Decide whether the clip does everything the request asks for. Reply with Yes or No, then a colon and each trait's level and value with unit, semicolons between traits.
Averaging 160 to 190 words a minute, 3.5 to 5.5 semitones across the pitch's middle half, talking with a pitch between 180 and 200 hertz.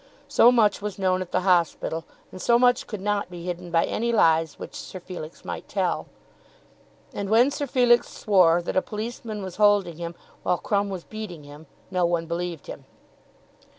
Yes: average, 185 wpm; average, 3.8 semitones; medium, 185 Hz